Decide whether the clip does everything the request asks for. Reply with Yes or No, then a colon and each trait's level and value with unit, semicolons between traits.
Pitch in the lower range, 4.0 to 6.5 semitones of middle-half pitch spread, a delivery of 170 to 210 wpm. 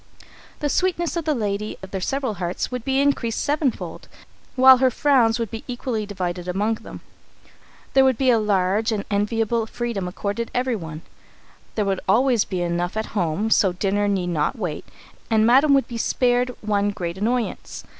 No: high, 220 Hz; average, 4.5 semitones; average, 175 wpm